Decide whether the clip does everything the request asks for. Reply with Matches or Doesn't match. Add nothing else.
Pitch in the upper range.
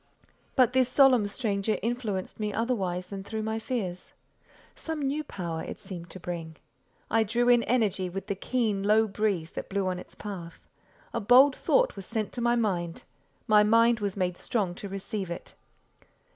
Matches